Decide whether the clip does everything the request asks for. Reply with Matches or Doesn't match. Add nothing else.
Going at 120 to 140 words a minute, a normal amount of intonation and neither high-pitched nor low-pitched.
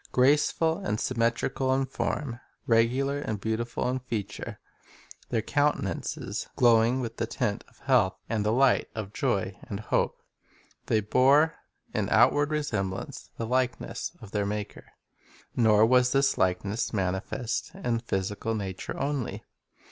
Doesn't match